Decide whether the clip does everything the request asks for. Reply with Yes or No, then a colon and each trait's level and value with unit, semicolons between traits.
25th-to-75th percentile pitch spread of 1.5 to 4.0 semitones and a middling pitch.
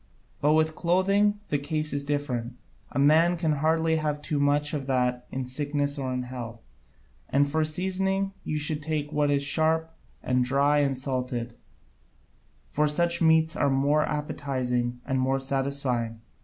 Yes: average, 3.1 semitones; medium, 145 Hz